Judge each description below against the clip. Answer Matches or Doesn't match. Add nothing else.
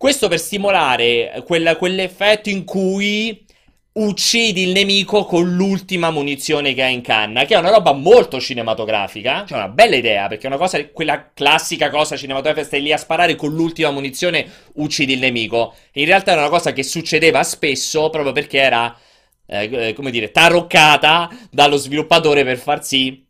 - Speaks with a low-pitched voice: Doesn't match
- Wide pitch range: Doesn't match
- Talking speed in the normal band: Doesn't match